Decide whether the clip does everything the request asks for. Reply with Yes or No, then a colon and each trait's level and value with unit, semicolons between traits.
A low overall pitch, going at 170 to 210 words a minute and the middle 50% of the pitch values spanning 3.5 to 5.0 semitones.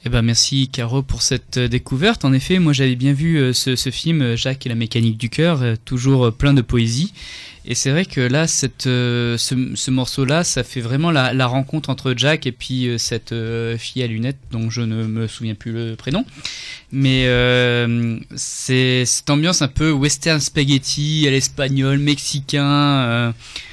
No: low, 130 Hz; average, 180 wpm; average, 3.1 semitones